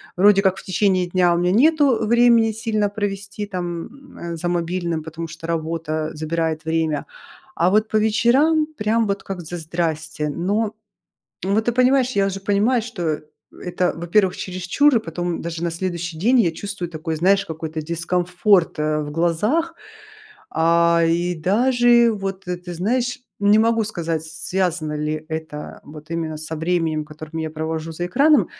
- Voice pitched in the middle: Yes, medium, 180 Hz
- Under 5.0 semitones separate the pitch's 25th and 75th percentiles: Yes, average, 4.5 semitones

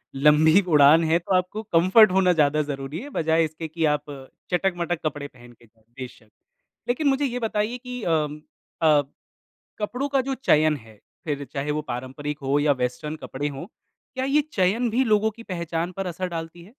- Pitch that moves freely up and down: Yes, wide, 5.9 semitones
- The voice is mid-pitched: Yes, medium, 165 Hz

